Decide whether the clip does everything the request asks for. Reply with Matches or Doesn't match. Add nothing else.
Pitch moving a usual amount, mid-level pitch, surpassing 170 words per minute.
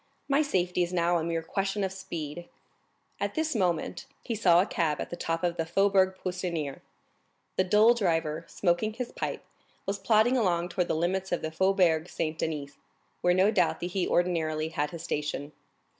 Matches